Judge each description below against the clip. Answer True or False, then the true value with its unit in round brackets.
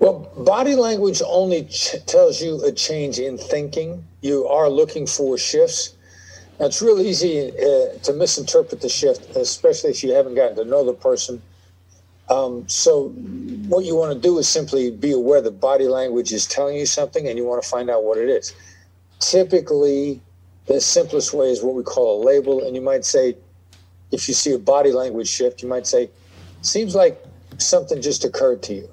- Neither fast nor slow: True (190 wpm)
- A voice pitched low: False (160 Hz)